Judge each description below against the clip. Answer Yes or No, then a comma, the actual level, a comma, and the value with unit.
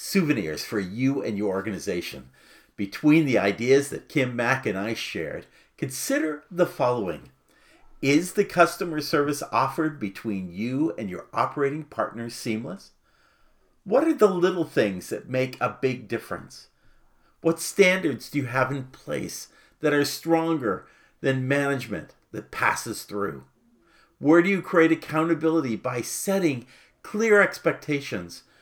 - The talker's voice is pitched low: No, medium, 145 Hz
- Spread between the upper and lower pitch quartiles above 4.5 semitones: Yes, average, 5.2 semitones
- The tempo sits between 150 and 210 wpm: No, slow, 135 wpm